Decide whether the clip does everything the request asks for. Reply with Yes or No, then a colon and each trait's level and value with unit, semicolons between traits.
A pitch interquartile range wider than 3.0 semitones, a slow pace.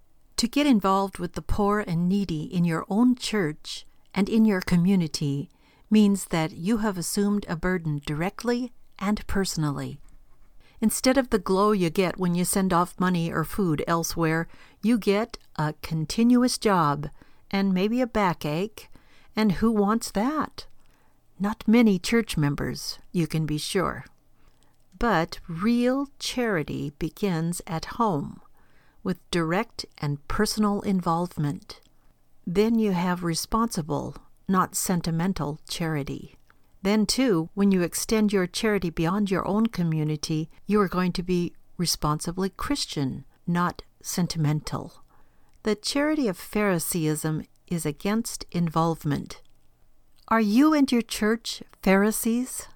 Yes: average, 4.5 semitones; slow, 125 wpm